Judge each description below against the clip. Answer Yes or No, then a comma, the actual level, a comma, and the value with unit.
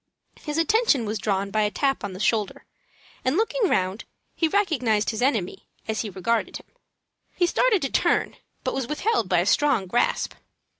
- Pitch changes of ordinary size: No, wide, 7.5 semitones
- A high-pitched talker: Yes, high, 235 Hz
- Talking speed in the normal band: Yes, average, 180 wpm